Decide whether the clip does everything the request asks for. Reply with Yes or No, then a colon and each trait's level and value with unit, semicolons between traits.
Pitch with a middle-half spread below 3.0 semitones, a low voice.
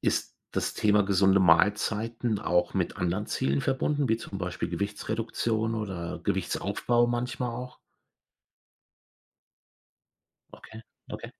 No: average, 3.6 semitones; low, 105 Hz